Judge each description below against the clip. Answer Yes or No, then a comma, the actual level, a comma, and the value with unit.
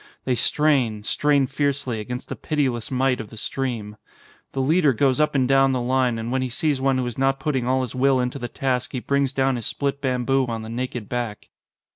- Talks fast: Yes, fast, 220 wpm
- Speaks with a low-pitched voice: Yes, low, 130 Hz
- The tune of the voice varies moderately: No, narrow, 1.9 semitones